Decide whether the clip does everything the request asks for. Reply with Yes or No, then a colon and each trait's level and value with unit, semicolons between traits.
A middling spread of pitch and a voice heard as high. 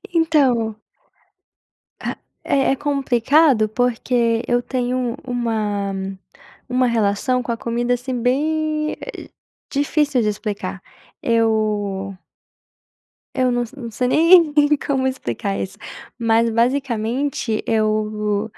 Yes: average, 3.6 semitones; high, 240 Hz